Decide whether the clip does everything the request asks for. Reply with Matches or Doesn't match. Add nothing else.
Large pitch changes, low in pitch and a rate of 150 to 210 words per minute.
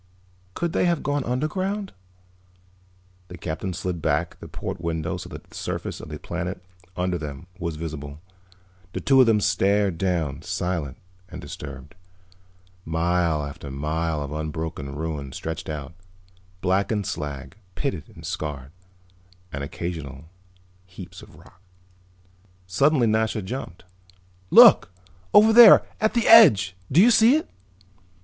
Doesn't match